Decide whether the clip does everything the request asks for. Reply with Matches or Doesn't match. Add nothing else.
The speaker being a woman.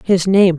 Matches